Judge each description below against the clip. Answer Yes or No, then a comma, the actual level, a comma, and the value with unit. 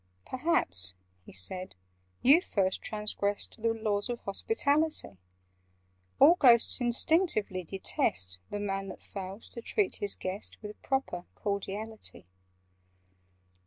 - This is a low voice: No, high, 210 Hz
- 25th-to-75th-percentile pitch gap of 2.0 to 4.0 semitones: No, average, 4.4 semitones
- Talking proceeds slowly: Yes, slow, 110 wpm